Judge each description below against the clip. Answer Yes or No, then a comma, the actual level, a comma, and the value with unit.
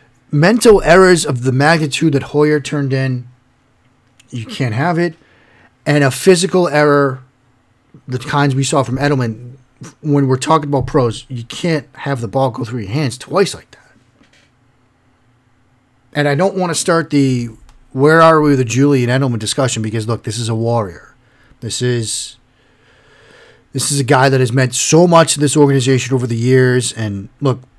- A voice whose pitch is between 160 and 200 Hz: No, low, 130 Hz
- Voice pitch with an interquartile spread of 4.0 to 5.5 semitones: No, average, 2.9 semitones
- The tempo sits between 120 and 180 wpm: Yes, average, 170 wpm